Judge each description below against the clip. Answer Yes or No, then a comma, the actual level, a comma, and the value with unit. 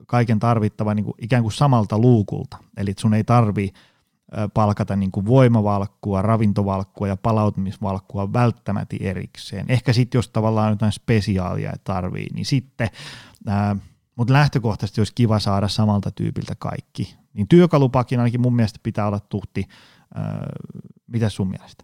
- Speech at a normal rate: Yes, average, 135 wpm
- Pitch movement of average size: Yes, average, 3.3 semitones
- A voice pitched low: Yes, low, 110 Hz